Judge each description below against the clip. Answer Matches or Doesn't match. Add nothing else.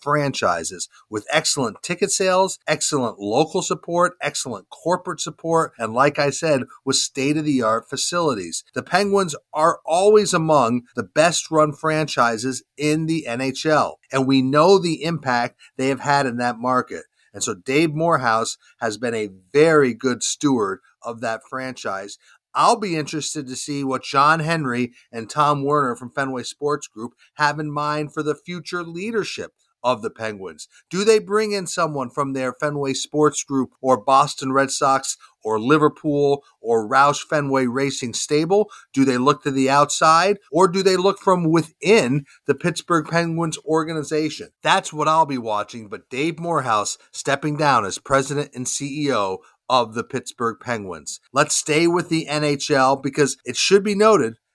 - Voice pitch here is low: Doesn't match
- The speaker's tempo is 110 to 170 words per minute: Matches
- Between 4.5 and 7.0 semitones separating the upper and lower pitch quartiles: Doesn't match